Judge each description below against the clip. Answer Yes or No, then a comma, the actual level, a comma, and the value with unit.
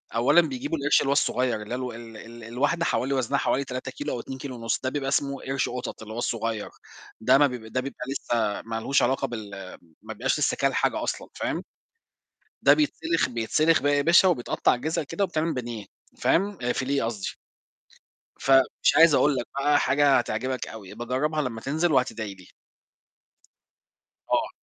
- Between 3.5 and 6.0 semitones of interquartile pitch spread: Yes, average, 3.9 semitones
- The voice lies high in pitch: No, low, 130 Hz